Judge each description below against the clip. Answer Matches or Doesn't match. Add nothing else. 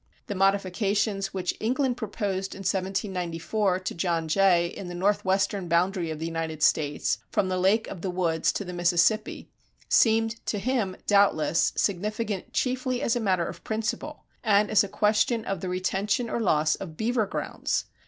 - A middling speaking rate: Matches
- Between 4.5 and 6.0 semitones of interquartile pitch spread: Doesn't match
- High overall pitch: Matches